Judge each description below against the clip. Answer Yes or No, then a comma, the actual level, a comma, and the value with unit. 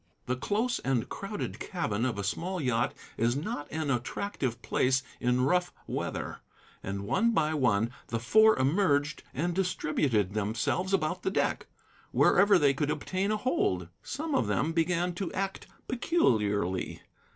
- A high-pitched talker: No, medium, 150 Hz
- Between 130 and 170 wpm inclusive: Yes, average, 150 wpm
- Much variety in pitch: Yes, wide, 8.0 semitones